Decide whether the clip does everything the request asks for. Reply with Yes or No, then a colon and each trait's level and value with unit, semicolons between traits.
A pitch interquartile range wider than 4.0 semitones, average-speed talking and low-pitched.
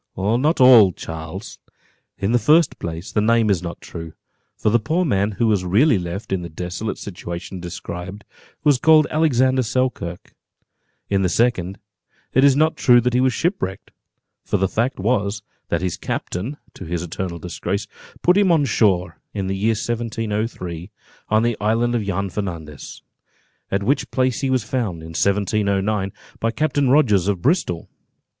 Yes: wide, 5.4 semitones; average, 165 wpm; low, 105 Hz